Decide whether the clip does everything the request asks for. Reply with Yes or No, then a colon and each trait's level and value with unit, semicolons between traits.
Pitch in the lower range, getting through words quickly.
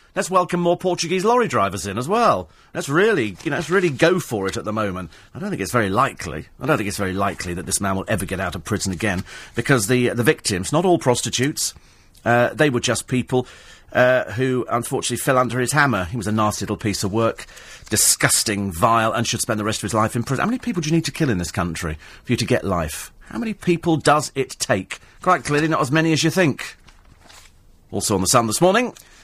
Yes: low, 120 Hz; fast, 240 wpm